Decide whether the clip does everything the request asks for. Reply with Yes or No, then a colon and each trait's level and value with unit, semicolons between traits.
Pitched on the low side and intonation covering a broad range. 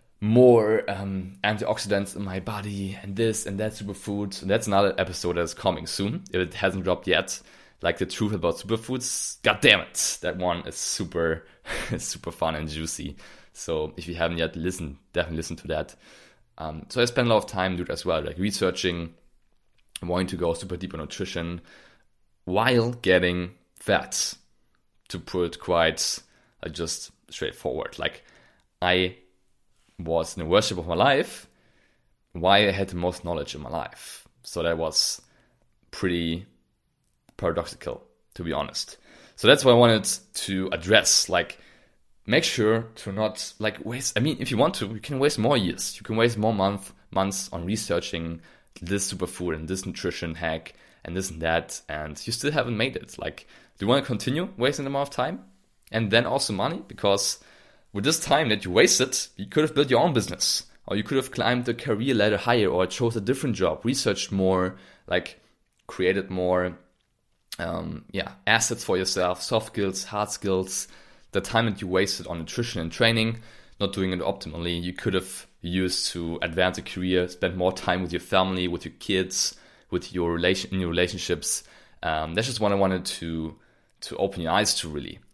No: very low, 95 Hz; average, 3.6 semitones